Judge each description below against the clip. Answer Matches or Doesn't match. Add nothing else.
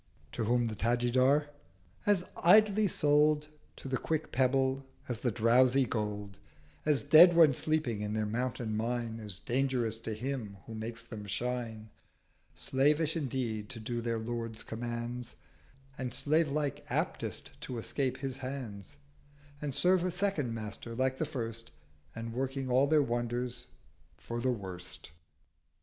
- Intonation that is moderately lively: Matches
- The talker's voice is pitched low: Matches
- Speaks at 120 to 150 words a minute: Matches